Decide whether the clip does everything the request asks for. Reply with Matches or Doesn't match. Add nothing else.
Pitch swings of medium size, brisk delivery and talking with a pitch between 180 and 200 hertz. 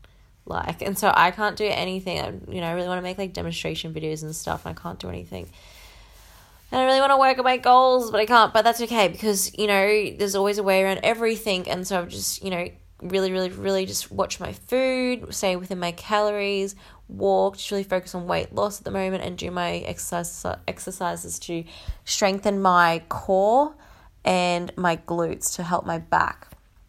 Matches